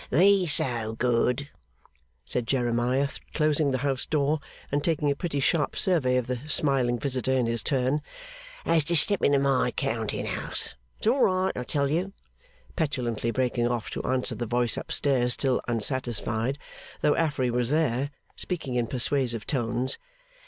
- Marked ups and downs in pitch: No, average, 3.3 semitones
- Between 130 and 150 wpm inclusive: No, average, 160 wpm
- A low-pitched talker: Yes, low, 130 Hz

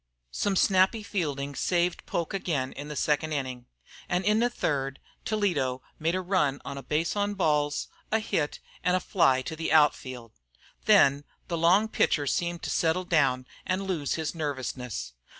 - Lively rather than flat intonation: No, average, 4.9 semitones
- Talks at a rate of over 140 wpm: Yes, average, 170 wpm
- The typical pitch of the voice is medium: Yes, medium, 160 Hz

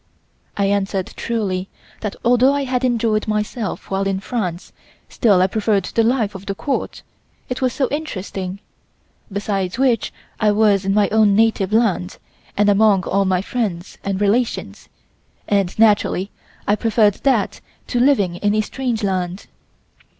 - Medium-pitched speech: No, high, 205 Hz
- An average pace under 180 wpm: Yes, average, 150 wpm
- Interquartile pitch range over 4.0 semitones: No, average, 2.9 semitones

